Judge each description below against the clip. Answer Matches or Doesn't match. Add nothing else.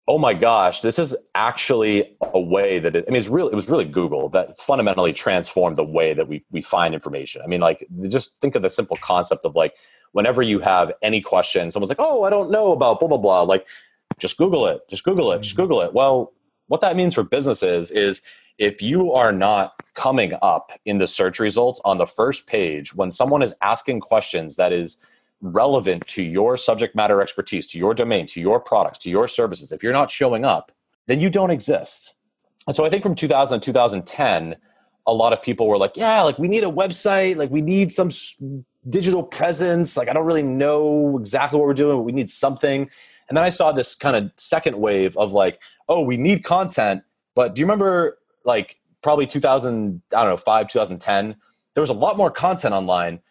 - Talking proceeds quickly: Matches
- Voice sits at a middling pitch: Matches